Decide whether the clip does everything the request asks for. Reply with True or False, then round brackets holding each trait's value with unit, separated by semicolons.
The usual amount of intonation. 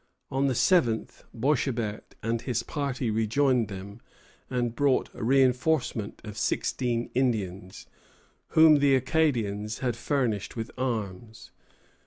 True (3.6 semitones)